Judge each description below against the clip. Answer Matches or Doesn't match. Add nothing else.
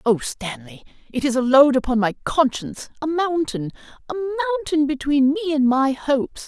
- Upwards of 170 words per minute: Doesn't match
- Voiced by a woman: Matches